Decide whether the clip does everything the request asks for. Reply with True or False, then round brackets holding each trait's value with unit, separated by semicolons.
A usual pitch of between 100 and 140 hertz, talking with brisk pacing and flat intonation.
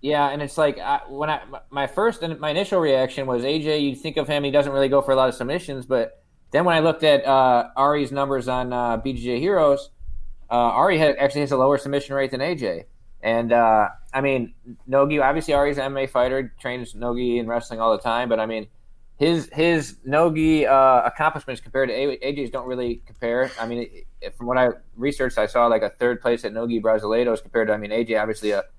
False (135 Hz; 225 wpm; 3.0 semitones)